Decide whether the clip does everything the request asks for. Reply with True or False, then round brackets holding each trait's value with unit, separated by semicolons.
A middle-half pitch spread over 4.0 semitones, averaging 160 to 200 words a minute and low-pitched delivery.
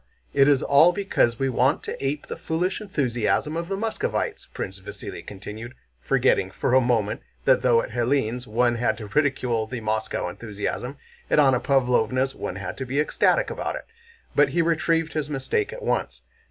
True (4.7 semitones; 180 wpm; 130 Hz)